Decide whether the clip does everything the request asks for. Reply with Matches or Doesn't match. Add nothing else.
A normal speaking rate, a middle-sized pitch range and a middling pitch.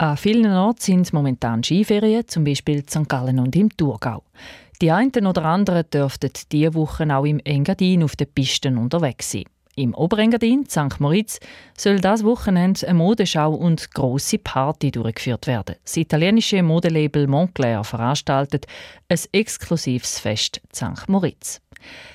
Doesn't match